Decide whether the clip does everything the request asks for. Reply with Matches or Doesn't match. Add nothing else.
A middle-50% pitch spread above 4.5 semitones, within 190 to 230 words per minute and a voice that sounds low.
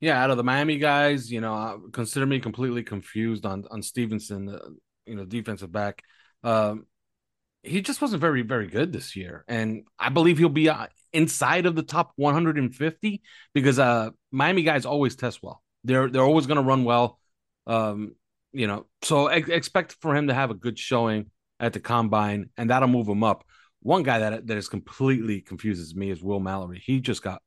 Matches